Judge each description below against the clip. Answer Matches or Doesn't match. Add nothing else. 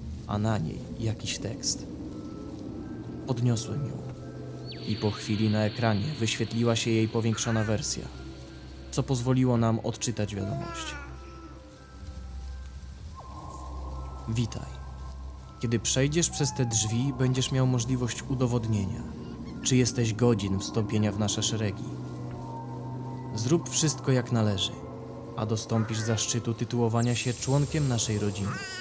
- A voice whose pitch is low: Matches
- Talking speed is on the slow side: Matches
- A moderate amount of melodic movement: Doesn't match